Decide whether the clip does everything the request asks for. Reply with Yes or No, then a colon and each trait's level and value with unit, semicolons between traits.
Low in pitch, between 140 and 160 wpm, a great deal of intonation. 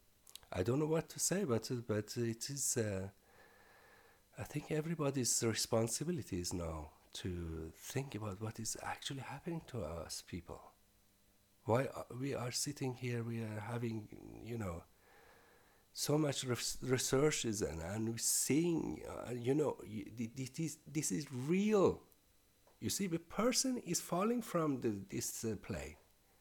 Yes: low, 115 Hz; average, 150 wpm; wide, 6.6 semitones